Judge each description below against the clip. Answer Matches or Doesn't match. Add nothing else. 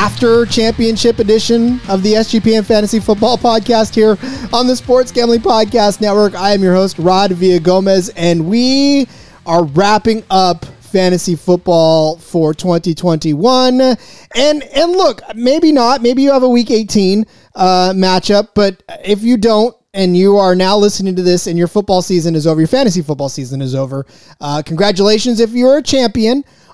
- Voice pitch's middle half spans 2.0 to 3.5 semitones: Doesn't match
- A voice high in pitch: Matches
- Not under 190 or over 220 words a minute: Doesn't match